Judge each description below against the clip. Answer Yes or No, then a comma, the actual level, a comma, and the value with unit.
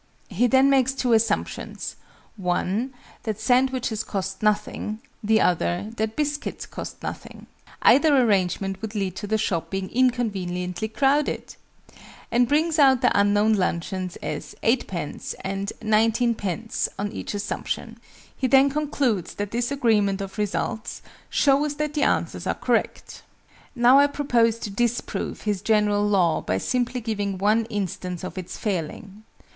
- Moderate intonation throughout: Yes, average, 4.3 semitones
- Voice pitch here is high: Yes, high, 215 Hz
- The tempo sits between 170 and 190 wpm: No, average, 140 wpm